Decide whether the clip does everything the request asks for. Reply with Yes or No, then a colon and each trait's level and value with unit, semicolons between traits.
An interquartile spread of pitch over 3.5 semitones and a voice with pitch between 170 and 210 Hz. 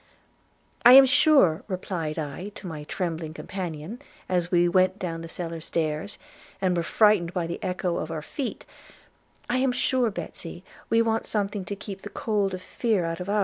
Yes: average, 4.0 semitones; medium, 185 Hz